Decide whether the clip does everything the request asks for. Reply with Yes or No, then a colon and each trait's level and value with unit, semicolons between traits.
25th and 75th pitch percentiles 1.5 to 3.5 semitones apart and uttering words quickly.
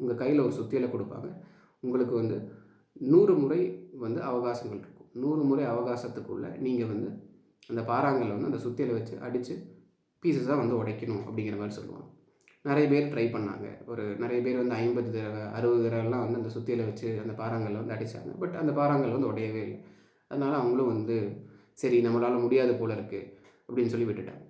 Yes: narrow, 2.6 semitones; fast, 165 wpm